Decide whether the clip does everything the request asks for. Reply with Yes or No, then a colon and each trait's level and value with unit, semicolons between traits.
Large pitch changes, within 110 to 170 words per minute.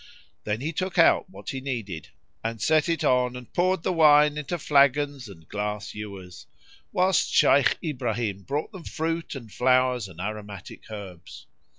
Yes: wide, 6.5 semitones; average, 160 wpm